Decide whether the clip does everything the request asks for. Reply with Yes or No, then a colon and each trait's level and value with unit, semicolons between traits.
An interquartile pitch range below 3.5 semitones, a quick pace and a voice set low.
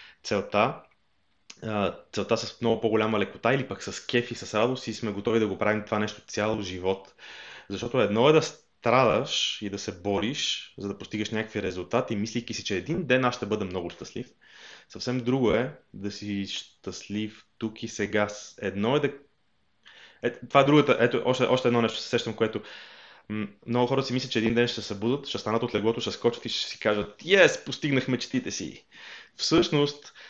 Yes: average, 2.9 semitones; fast, 190 wpm; low, 110 Hz